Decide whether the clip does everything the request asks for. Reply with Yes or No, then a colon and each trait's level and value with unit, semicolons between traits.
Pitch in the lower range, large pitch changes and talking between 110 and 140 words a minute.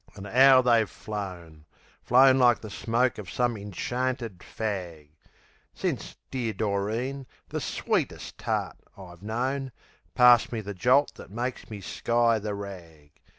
No: low, 110 Hz; average, 4.0 semitones; slow, 135 wpm